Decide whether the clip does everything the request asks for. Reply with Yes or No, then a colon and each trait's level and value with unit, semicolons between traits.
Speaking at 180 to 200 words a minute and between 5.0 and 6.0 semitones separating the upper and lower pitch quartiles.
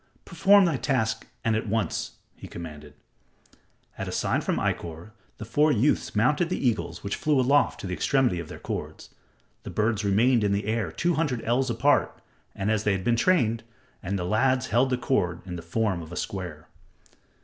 Yes: average, 185 wpm; average, 5.3 semitones